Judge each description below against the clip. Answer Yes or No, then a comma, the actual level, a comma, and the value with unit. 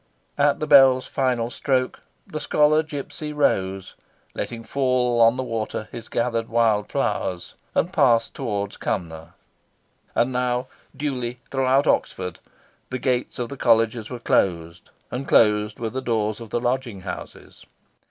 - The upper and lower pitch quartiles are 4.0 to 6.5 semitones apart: No, average, 3.3 semitones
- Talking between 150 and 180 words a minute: No, average, 140 wpm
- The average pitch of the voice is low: Yes, low, 120 Hz